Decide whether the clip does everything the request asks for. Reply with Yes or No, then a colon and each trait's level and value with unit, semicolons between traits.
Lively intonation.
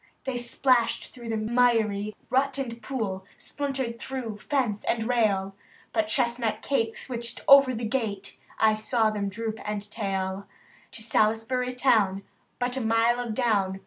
No: average, 2.7 semitones